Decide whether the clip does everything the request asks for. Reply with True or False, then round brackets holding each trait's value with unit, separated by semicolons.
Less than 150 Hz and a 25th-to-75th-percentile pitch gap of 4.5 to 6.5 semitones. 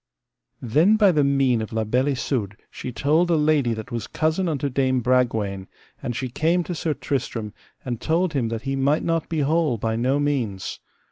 True (135 Hz; 5.0 semitones)